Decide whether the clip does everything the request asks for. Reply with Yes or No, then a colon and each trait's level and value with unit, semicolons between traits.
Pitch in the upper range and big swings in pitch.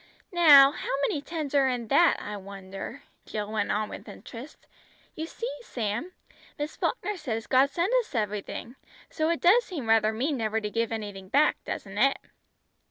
Yes: very high, 255 Hz; wide, 6.5 semitones